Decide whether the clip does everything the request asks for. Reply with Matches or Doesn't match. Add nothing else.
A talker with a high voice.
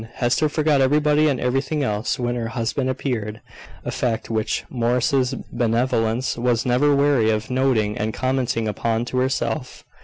Doesn't match